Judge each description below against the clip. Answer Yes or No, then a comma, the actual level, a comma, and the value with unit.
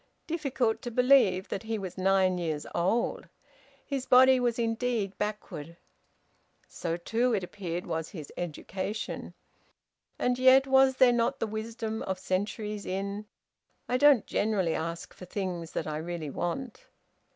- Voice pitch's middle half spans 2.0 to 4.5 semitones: No, average, 5.3 semitones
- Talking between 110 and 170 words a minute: Yes, average, 140 wpm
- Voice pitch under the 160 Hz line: No, high, 210 Hz